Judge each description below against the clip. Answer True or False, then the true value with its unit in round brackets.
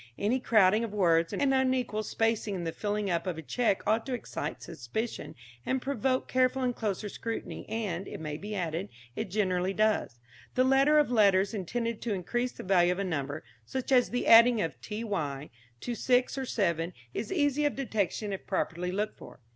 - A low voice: False (215 Hz)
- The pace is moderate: True (190 wpm)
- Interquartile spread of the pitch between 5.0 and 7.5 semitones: True (5.3 semitones)